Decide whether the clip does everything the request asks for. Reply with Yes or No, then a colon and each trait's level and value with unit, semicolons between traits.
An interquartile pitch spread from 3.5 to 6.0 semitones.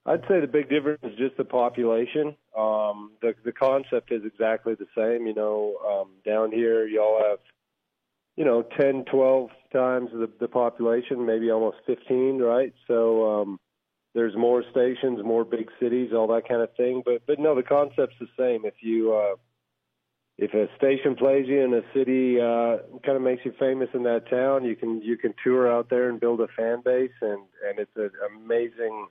No: average, 2.7 semitones